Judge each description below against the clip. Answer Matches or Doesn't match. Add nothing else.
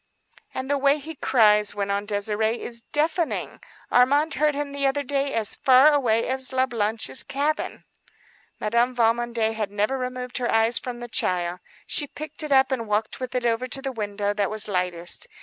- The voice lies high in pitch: Matches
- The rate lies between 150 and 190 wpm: Matches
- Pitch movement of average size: Matches